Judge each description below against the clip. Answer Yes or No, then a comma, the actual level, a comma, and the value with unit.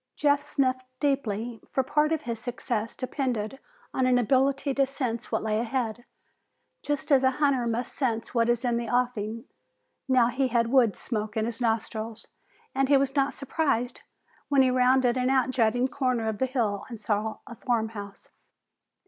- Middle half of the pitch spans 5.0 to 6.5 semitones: No, average, 2.8 semitones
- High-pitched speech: Yes, very high, 250 Hz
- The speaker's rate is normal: Yes, average, 175 wpm